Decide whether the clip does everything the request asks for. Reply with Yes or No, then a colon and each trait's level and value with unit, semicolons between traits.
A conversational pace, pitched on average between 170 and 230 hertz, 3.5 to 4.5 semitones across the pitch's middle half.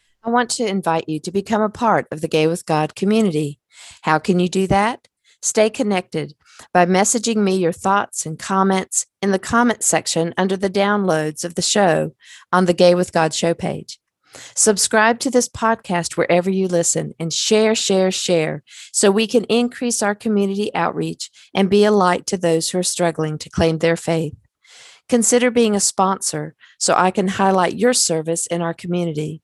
Yes: average, 185 wpm; high, 190 Hz; average, 4.1 semitones